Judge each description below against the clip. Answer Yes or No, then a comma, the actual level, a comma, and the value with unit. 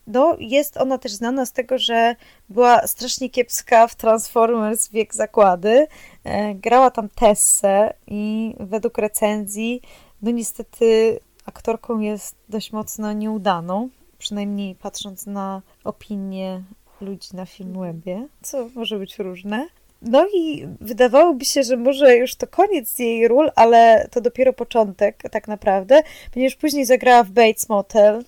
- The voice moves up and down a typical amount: Yes, average, 3.5 semitones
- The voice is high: Yes, high, 230 Hz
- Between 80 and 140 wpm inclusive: Yes, average, 130 wpm